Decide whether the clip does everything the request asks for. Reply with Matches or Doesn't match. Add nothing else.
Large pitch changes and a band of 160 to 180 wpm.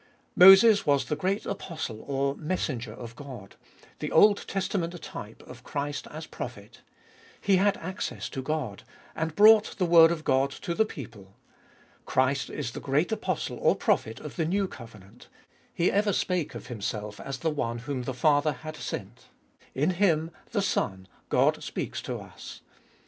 Matches